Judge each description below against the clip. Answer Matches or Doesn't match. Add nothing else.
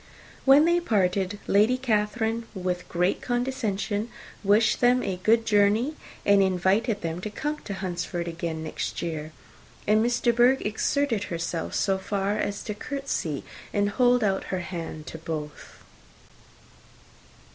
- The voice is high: Matches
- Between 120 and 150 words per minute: Matches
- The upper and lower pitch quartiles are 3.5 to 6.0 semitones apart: Matches